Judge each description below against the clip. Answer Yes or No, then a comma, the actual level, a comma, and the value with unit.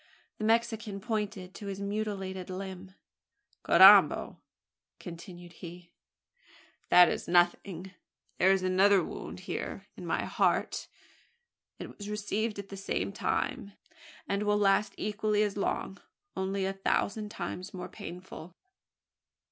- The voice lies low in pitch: No, high, 195 Hz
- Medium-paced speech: No, slow, 125 wpm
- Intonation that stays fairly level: Yes, narrow, 2.1 semitones